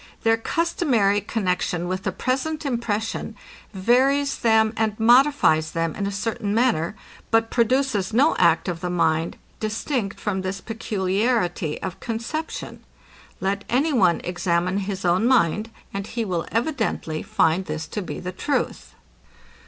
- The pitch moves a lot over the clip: No, average, 4.6 semitones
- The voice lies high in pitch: Yes, high, 210 Hz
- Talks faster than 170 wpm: No, average, 140 wpm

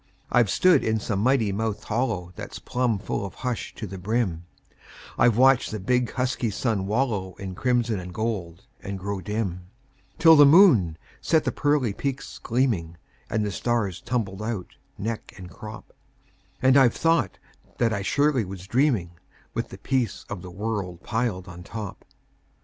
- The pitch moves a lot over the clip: No, average, 4.6 semitones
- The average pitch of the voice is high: No, low, 110 Hz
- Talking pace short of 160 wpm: No, average, 165 wpm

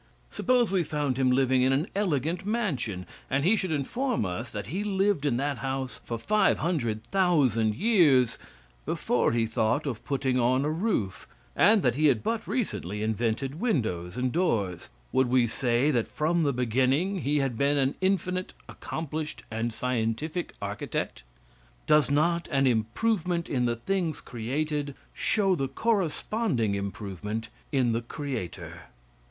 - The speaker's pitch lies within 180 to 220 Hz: No, low, 135 Hz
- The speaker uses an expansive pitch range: Yes, wide, 6.6 semitones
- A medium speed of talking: Yes, average, 150 wpm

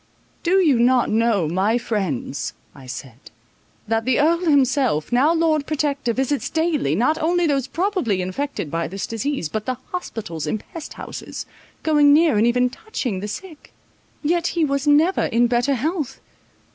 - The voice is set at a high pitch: Yes, very high, 260 Hz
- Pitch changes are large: Yes, wide, 6.4 semitones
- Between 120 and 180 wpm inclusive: Yes, average, 160 wpm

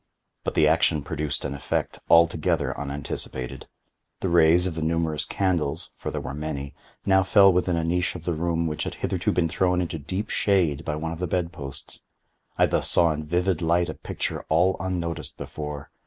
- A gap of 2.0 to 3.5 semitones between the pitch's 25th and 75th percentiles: Yes, average, 2.8 semitones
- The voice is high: No, very low, 85 Hz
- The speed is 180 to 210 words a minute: Yes, average, 190 wpm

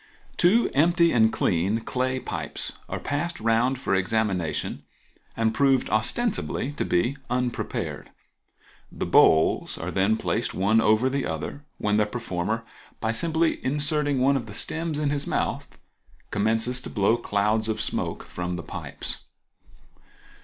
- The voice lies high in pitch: No, low, 115 Hz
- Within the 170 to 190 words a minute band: No, average, 140 wpm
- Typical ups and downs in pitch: Yes, average, 4.9 semitones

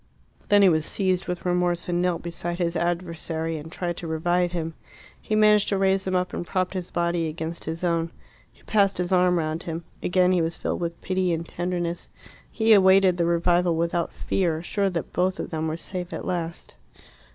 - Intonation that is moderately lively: No, narrow, 1.7 semitones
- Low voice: No, medium, 175 Hz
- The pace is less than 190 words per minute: No, average, 200 wpm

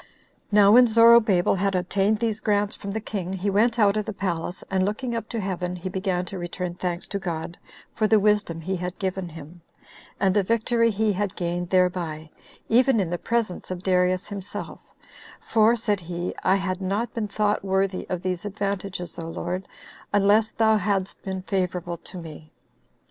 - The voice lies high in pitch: Yes, high, 195 Hz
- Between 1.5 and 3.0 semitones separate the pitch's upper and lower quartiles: Yes, average, 2.7 semitones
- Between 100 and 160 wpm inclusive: No, average, 185 wpm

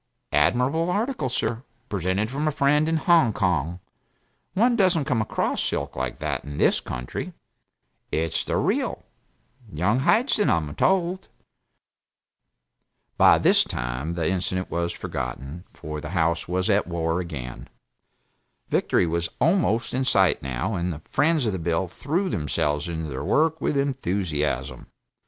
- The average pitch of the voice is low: Yes, very low, 95 Hz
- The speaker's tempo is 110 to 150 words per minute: Yes, average, 140 wpm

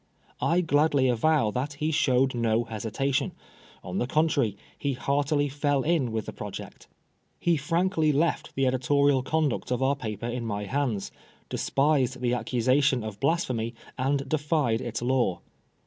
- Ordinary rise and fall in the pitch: Yes, average, 3.5 semitones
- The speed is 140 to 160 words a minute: Yes, average, 155 wpm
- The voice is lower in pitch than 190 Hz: Yes, low, 135 Hz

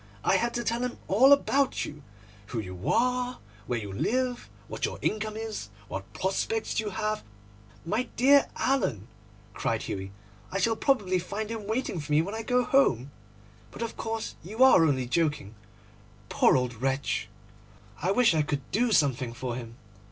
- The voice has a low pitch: No, high, 195 Hz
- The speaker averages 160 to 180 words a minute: Yes, average, 165 wpm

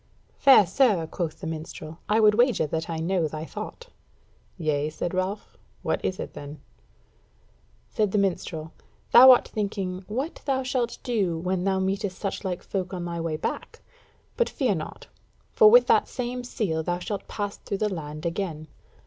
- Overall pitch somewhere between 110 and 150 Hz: No, high, 190 Hz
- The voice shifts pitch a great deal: No, average, 4.7 semitones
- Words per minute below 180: Yes, average, 170 wpm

